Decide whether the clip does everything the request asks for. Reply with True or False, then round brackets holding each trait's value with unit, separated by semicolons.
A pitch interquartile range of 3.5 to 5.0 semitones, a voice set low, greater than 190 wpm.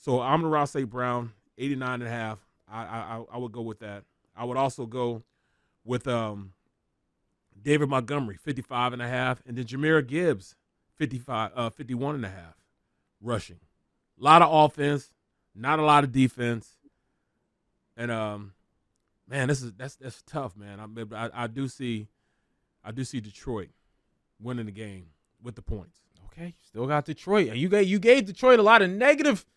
False (4.5 semitones; 125 Hz; 175 wpm)